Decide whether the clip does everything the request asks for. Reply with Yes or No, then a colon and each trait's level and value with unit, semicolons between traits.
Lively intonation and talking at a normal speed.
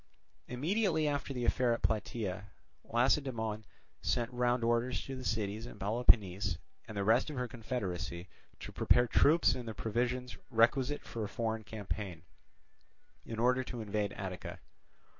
No: average, 2.9 semitones; average, 145 wpm